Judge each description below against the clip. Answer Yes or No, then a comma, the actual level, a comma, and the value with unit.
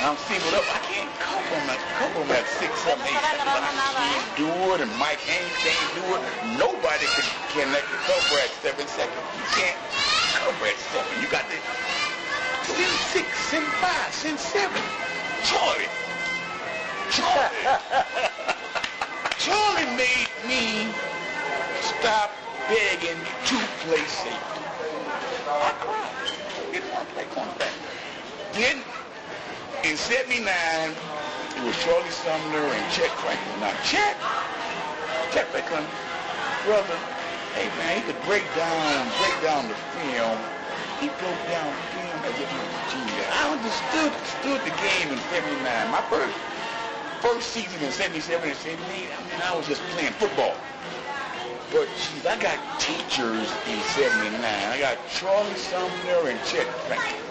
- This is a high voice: Yes, high, 245 Hz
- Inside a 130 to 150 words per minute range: Yes, average, 140 wpm